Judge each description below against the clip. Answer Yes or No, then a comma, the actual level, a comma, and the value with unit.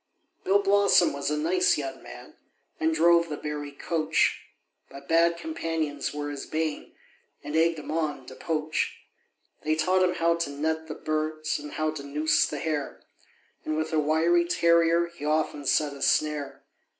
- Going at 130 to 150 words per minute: No, average, 170 wpm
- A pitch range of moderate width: No, narrow, 2.2 semitones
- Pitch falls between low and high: Yes, medium, 155 Hz